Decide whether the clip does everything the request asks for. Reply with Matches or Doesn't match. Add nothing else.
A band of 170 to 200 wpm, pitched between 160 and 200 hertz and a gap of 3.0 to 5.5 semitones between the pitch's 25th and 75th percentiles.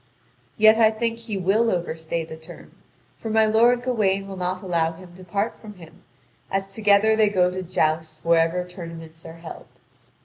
Matches